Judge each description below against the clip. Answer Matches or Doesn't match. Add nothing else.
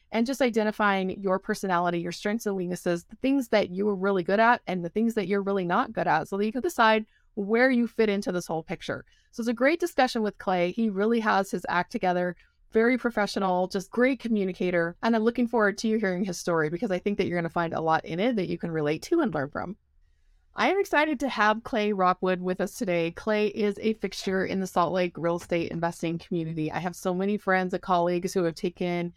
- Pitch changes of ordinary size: Matches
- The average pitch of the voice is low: Doesn't match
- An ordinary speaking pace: Doesn't match